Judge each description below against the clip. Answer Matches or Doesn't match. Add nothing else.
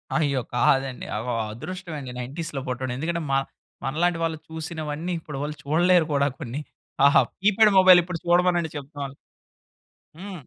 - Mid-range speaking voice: Matches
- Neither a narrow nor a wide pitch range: Matches